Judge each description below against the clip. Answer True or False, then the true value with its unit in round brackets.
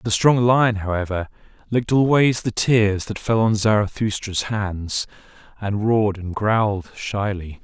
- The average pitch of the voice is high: False (105 Hz)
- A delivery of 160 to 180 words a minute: False (140 wpm)